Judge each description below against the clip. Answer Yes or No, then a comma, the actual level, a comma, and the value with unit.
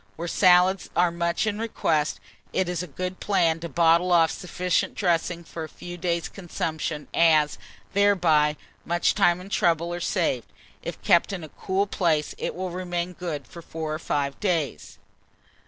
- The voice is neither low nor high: Yes, medium, 170 Hz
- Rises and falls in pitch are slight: Yes, narrow, 2.1 semitones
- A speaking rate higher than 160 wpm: Yes, average, 170 wpm